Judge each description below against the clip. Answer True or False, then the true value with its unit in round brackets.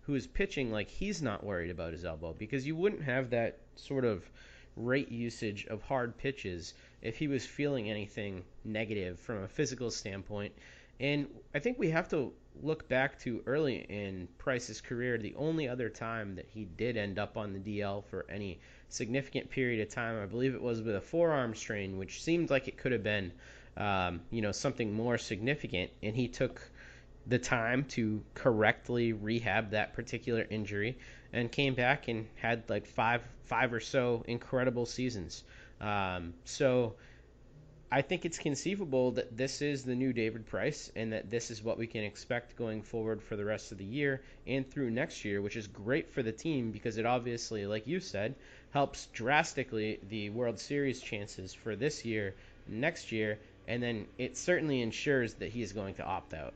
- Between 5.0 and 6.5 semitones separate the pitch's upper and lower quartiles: False (3.8 semitones)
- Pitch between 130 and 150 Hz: False (115 Hz)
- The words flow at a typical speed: True (185 wpm)